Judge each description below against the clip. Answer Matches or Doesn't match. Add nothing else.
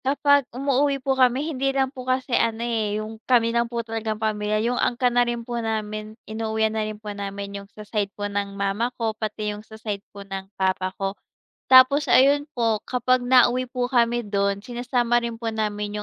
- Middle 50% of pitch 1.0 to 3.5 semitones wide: Matches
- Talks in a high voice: Matches